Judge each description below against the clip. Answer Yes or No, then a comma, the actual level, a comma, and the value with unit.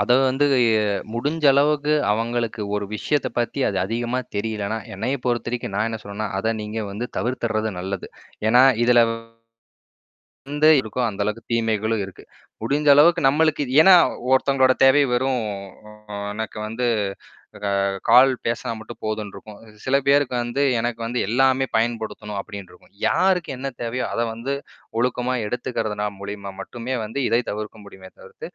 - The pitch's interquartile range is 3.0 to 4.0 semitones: Yes, average, 3.4 semitones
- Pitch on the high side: No, low, 120 Hz